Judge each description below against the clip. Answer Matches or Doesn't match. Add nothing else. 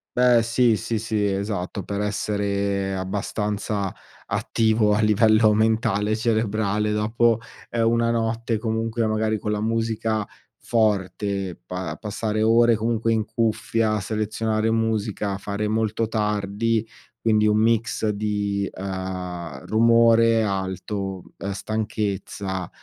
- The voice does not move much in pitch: Matches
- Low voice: Matches